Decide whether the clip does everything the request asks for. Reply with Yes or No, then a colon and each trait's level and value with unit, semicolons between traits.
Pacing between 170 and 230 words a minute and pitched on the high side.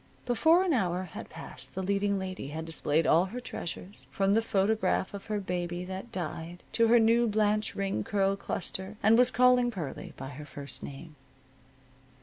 Yes: average, 175 wpm; high, 195 Hz